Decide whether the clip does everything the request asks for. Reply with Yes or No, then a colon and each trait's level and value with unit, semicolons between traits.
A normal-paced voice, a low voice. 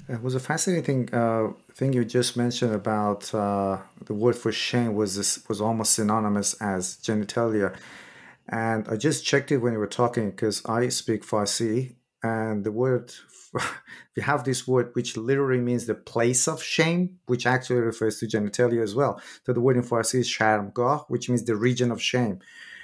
Yes: average, 185 wpm; low, 120 Hz